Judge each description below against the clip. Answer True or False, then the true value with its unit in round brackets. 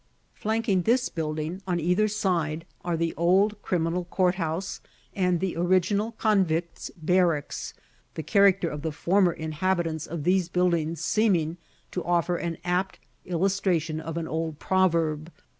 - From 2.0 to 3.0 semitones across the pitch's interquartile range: True (2.7 semitones)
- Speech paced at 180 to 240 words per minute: False (135 wpm)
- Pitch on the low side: False (175 Hz)